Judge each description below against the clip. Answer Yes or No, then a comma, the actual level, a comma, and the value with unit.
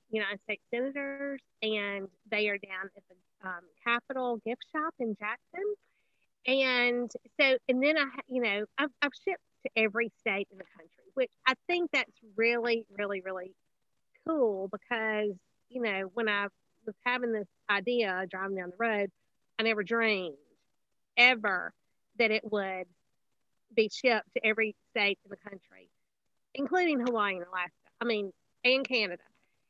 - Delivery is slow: No, average, 150 wpm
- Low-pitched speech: No, high, 225 Hz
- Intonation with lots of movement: No, average, 4.1 semitones